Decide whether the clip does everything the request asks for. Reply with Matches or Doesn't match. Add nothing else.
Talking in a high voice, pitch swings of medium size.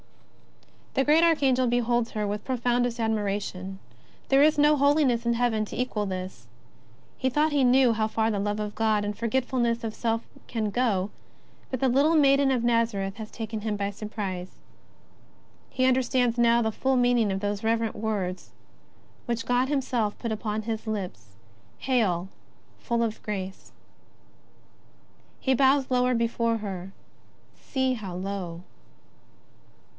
Matches